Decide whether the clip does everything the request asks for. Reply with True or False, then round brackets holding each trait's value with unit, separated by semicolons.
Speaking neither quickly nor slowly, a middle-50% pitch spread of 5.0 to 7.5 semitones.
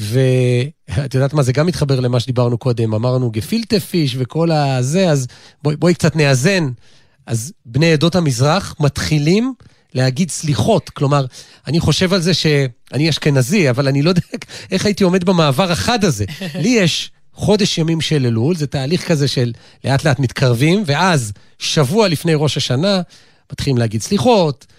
False (155 wpm; 5.5 semitones)